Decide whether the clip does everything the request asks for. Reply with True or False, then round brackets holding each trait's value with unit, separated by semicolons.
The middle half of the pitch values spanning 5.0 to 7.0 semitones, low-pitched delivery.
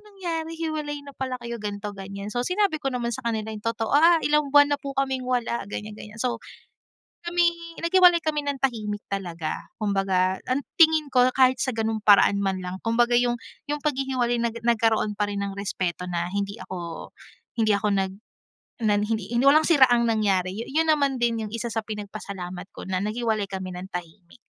False (5.3 semitones; 230 Hz)